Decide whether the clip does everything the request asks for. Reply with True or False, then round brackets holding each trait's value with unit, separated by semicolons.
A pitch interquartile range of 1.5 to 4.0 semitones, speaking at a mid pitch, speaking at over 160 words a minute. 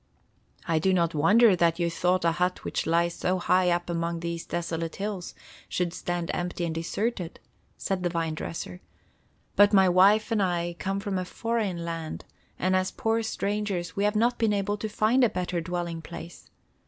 True (3.1 semitones; 180 Hz; 185 wpm)